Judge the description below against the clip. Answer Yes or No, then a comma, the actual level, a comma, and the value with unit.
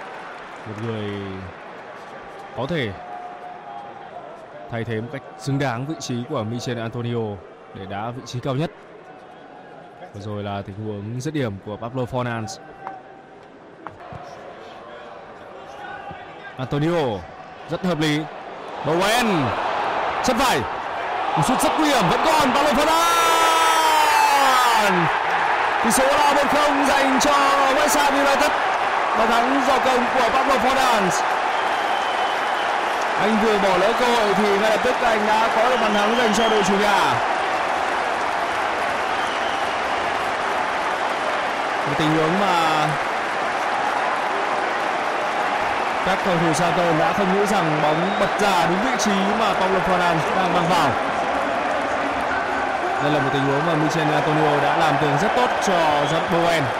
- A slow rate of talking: Yes, slow, 130 wpm